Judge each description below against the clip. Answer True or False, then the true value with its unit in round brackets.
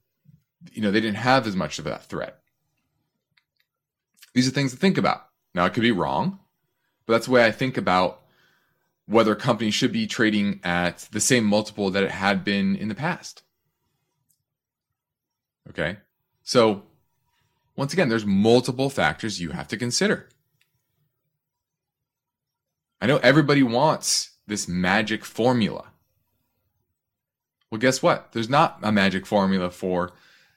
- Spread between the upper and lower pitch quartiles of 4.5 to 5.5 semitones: True (4.8 semitones)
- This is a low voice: True (115 Hz)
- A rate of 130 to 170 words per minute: True (140 wpm)